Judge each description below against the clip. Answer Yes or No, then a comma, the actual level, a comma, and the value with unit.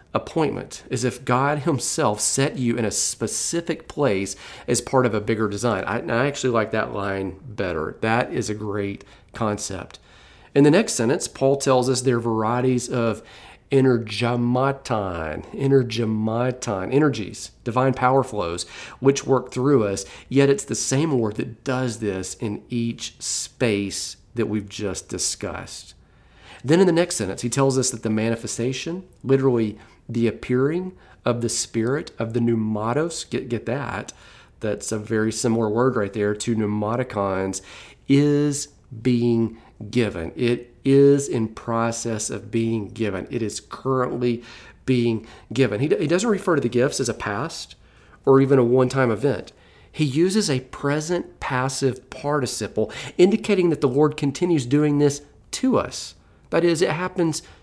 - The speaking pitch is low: Yes, low, 120 Hz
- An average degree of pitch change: Yes, average, 3.9 semitones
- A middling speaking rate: Yes, average, 155 wpm